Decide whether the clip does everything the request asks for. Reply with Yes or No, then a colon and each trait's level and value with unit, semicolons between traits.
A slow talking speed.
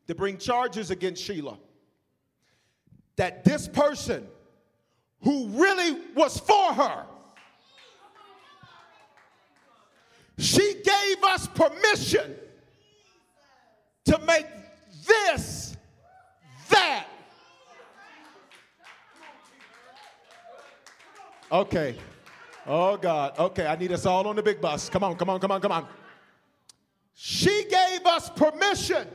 Yes: slow, 95 wpm